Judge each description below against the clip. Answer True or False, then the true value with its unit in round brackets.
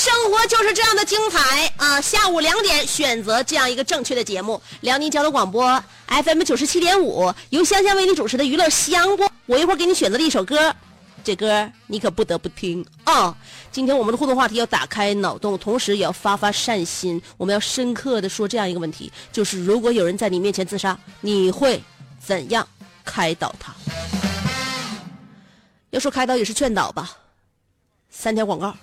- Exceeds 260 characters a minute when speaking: True (295 characters per minute)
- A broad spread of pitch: True (6.8 semitones)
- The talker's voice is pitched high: True (230 Hz)